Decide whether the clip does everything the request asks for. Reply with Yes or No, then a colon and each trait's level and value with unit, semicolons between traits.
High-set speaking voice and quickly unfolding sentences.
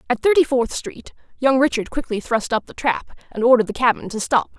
Yes: high, 245 Hz; fast, 225 wpm